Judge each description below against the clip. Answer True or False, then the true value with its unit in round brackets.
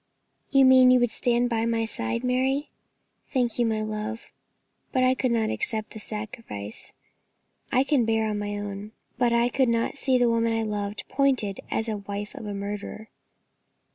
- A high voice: True (230 Hz)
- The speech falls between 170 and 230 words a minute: True (185 wpm)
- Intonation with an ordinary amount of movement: True (3.0 semitones)